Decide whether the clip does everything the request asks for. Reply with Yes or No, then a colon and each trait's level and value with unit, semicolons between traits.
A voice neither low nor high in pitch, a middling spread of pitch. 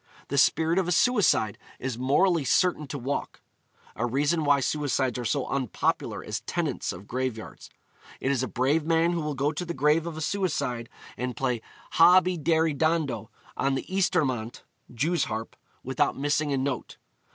Yes: medium, 145 Hz; average, 4.3 semitones